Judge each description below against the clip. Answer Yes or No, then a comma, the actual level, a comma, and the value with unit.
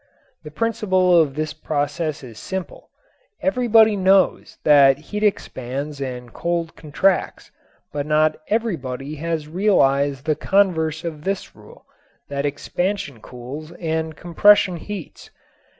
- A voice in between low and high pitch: Yes, medium, 160 Hz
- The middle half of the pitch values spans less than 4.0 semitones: No, average, 4.7 semitones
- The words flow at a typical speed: No, slow, 120 wpm